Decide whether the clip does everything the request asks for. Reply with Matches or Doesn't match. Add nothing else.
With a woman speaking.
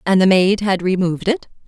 Matches